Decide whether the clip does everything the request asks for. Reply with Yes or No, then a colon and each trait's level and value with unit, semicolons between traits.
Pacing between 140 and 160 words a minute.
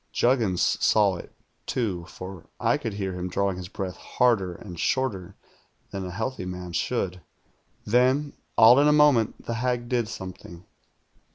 Yes: average, 155 wpm